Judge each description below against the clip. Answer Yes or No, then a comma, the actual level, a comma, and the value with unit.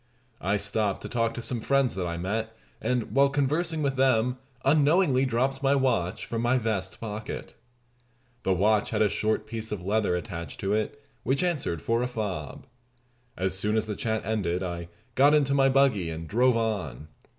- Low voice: Yes, low, 110 Hz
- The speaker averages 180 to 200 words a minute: Yes, average, 185 wpm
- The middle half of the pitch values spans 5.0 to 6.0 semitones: Yes, wide, 5.4 semitones